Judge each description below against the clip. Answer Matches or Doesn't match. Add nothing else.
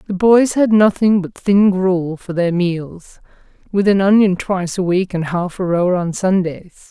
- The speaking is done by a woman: Matches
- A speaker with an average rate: Matches